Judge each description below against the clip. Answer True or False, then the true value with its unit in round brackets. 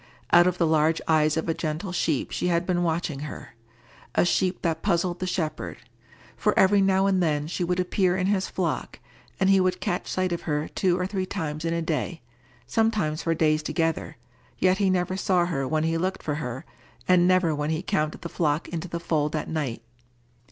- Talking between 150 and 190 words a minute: False (205 wpm)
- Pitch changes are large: False (3.0 semitones)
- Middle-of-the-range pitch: True (170 Hz)